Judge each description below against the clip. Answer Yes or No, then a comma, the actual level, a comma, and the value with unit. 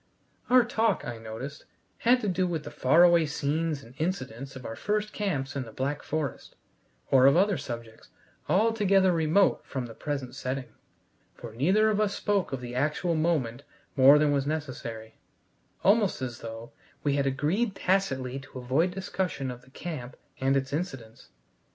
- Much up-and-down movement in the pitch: Yes, wide, 6.1 semitones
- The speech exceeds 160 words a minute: Yes, average, 170 wpm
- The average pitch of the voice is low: No, medium, 145 Hz